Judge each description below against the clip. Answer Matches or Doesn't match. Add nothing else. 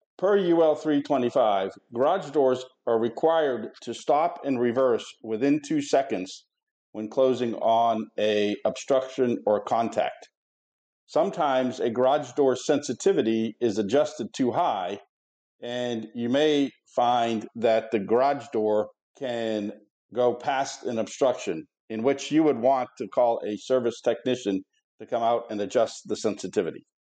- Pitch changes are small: Doesn't match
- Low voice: Matches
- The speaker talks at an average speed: Doesn't match